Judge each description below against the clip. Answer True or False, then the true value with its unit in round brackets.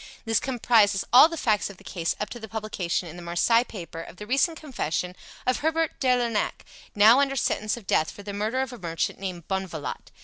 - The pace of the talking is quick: True (215 wpm)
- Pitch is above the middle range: True (215 Hz)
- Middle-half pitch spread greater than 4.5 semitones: True (5.4 semitones)